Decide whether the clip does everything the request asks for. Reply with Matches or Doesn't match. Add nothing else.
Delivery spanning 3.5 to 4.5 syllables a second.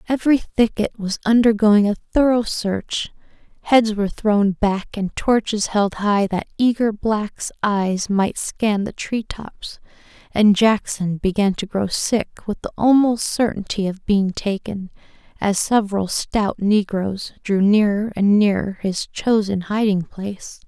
Matches